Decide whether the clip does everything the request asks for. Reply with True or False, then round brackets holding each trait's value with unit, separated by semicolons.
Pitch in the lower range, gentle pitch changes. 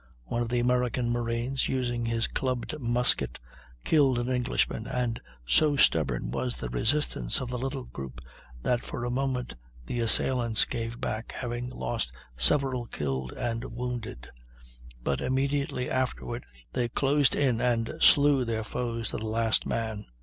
True (120 Hz; 2.1 semitones)